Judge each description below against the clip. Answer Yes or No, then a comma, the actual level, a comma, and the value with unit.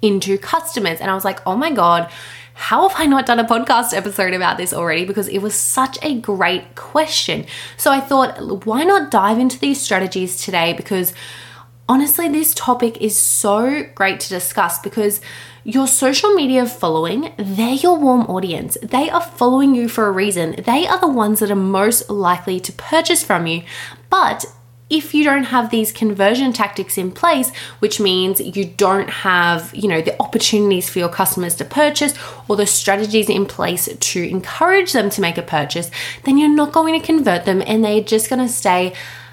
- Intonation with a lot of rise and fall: Yes, wide, 5.9 semitones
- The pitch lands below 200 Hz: No, high, 210 Hz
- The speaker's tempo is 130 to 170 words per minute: No, average, 190 wpm